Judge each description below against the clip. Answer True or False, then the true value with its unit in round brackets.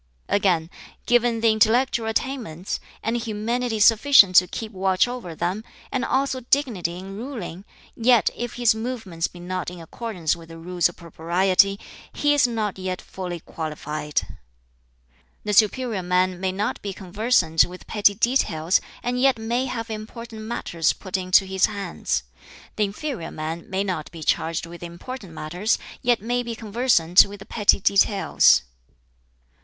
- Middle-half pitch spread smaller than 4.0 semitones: False (4.8 semitones)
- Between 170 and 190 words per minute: False (150 wpm)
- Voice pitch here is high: True (200 Hz)